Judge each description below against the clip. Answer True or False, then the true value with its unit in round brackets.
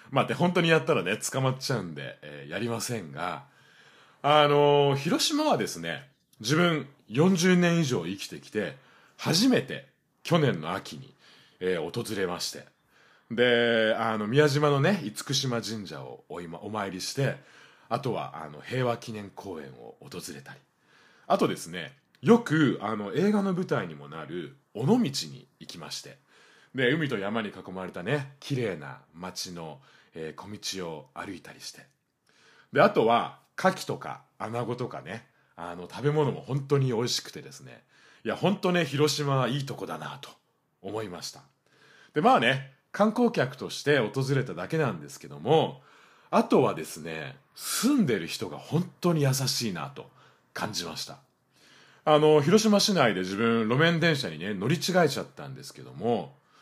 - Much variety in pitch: True (5.8 semitones)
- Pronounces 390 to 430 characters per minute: False (290 characters per minute)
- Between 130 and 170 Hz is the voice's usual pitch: True (140 Hz)